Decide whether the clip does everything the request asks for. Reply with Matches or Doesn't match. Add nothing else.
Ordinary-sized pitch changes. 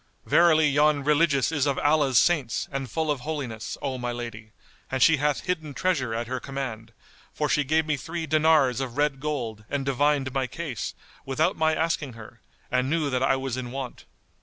Matches